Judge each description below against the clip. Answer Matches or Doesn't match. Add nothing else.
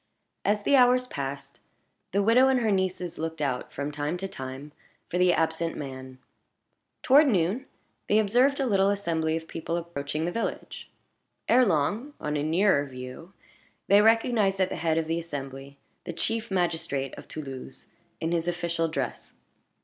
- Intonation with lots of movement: Matches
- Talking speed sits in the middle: Matches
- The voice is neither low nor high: Matches